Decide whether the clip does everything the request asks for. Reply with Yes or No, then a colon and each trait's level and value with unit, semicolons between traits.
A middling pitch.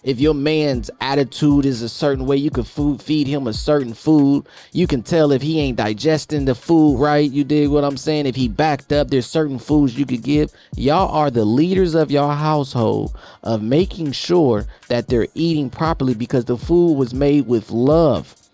Yes: medium, 145 Hz